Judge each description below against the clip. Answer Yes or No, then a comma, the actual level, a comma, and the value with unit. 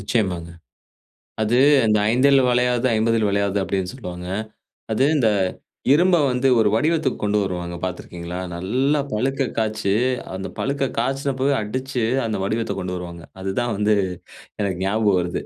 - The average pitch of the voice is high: No, low, 110 Hz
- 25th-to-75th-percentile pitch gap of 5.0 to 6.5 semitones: Yes, average, 5.3 semitones